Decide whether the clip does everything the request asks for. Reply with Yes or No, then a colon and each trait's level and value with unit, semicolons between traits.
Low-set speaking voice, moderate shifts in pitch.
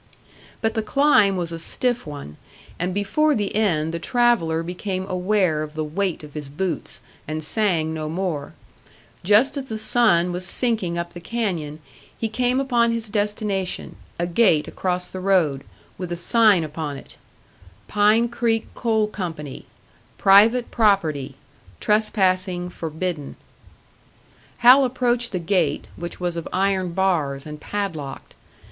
No: medium, 185 Hz; average, 5.0 semitones